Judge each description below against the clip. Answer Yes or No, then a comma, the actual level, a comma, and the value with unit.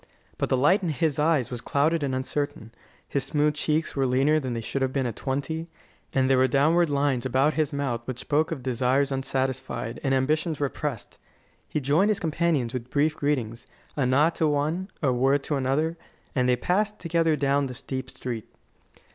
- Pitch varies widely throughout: No, average, 3.0 semitones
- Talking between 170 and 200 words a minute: Yes, average, 190 wpm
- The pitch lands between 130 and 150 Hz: Yes, medium, 140 Hz